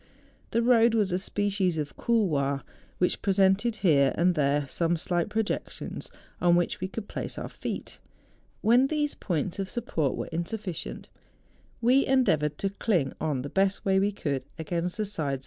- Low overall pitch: No, medium, 185 Hz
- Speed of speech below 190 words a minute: Yes, average, 175 wpm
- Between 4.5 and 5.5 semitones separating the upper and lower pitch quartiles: Yes, average, 5.2 semitones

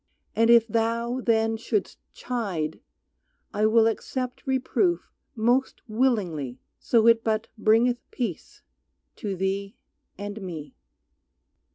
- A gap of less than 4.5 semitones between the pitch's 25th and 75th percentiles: Yes, average, 2.8 semitones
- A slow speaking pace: Yes, slow, 105 wpm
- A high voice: Yes, high, 225 Hz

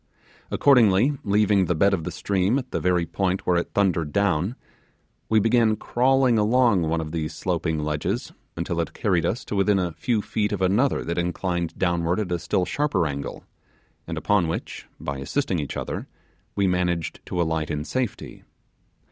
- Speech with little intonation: No, average, 4.1 semitones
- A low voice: Yes, very low, 95 Hz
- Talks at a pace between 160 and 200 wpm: Yes, average, 175 wpm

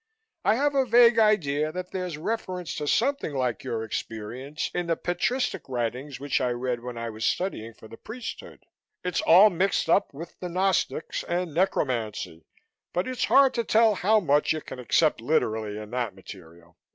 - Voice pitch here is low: No, medium, 155 Hz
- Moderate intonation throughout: No, wide, 8.4 semitones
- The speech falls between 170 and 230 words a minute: Yes, average, 175 wpm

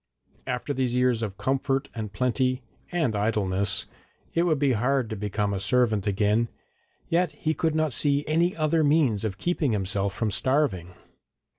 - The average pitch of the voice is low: Yes, low, 125 Hz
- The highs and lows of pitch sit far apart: Yes, wide, 5.8 semitones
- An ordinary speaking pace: Yes, average, 160 wpm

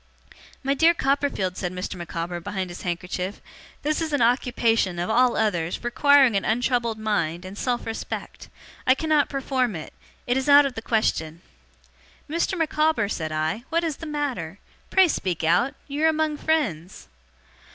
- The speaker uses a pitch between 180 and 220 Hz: No, high, 235 Hz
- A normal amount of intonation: No, wide, 7.9 semitones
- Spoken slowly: No, average, 160 wpm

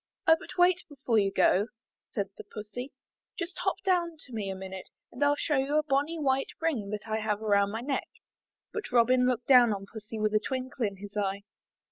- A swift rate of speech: Yes, fast, 210 wpm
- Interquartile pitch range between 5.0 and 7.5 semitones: Yes, wide, 5.5 semitones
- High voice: Yes, high, 240 Hz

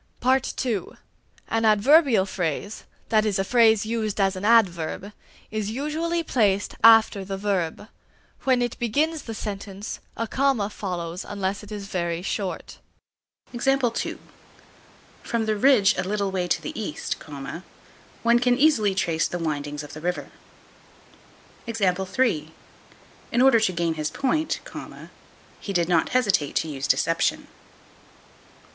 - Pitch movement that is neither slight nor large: Yes, average, 4.3 semitones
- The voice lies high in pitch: Yes, high, 205 Hz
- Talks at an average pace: No, slow, 130 wpm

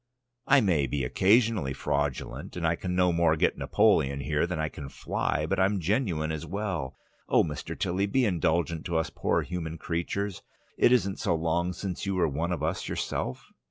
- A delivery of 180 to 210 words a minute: Yes, average, 190 wpm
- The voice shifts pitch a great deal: No, average, 3.8 semitones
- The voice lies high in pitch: No, very low, 85 Hz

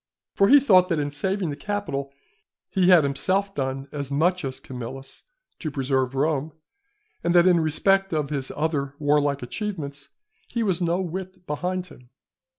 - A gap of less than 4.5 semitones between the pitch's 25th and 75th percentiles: No, average, 4.9 semitones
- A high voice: No, medium, 155 Hz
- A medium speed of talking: Yes, average, 160 wpm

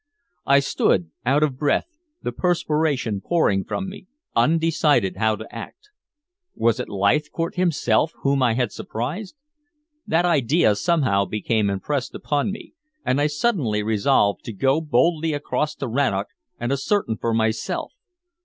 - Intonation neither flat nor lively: No, wide, 6.2 semitones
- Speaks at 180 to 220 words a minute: No, average, 140 wpm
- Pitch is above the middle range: No, medium, 140 Hz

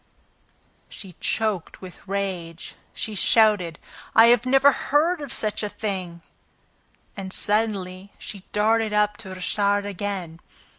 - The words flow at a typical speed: No, slow, 115 wpm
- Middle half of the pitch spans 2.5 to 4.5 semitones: Yes, average, 2.8 semitones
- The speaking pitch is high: Yes, high, 205 Hz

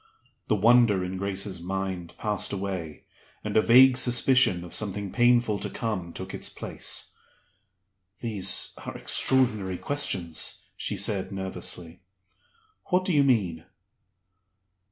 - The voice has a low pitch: Yes, low, 100 Hz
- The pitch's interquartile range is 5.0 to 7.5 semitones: No, average, 4.6 semitones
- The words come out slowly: Yes, slow, 120 wpm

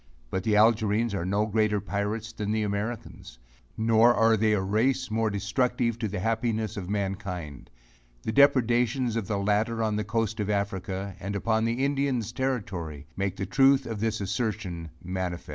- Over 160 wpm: Yes, average, 170 wpm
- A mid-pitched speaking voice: No, low, 110 Hz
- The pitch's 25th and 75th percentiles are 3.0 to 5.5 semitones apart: No, narrow, 2.6 semitones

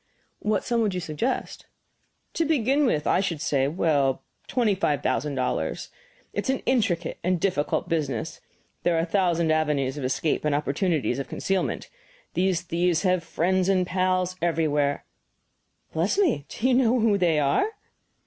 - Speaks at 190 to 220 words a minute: No, average, 165 wpm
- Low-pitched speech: No, medium, 175 Hz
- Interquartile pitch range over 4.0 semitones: Yes, average, 4.8 semitones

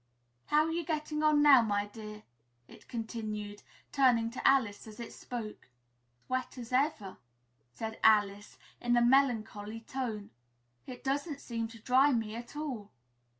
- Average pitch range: Yes, average, 4.1 semitones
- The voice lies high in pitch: Yes, high, 235 Hz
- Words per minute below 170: Yes, average, 150 wpm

